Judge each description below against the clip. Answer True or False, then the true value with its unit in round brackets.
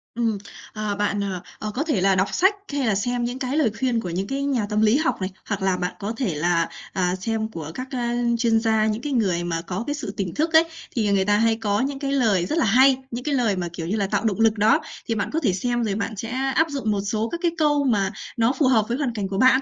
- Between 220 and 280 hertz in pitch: True (225 Hz)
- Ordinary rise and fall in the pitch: True (4.7 semitones)